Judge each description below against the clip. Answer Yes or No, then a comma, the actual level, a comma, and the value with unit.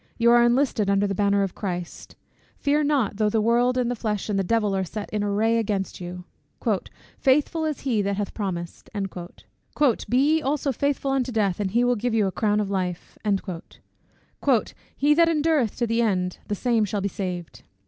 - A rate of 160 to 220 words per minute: Yes, average, 190 wpm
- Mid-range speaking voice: No, high, 215 Hz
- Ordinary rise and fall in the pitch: Yes, average, 4.1 semitones